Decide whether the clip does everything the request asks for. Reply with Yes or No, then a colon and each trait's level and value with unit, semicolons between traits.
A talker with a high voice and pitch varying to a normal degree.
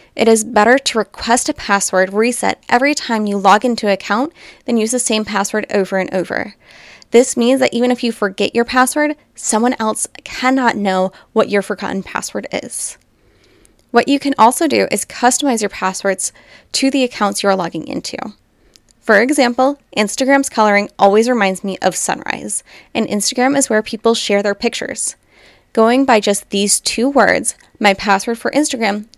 Yes: high, 225 Hz; average, 3.8 semitones